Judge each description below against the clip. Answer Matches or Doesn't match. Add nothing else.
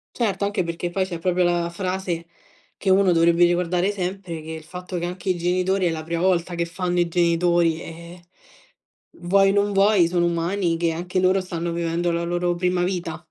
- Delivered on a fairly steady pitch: Matches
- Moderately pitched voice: Matches